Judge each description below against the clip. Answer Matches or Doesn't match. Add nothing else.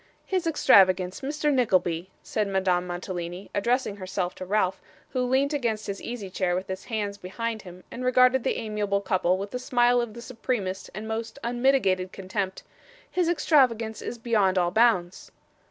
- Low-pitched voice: Doesn't match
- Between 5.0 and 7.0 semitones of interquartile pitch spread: Doesn't match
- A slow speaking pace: Doesn't match